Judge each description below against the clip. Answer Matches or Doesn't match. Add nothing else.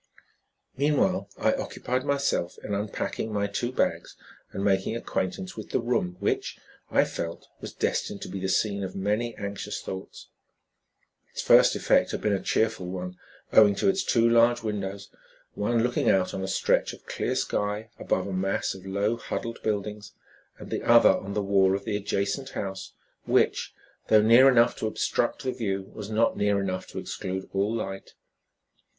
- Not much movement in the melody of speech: Doesn't match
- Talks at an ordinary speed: Matches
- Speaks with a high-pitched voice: Doesn't match